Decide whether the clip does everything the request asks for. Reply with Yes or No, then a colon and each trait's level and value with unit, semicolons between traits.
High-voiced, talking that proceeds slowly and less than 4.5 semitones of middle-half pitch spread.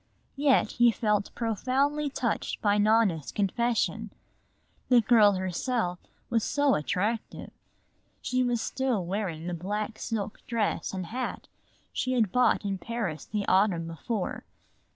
Yes: high, 215 Hz; slow, 130 wpm; average, 4.1 semitones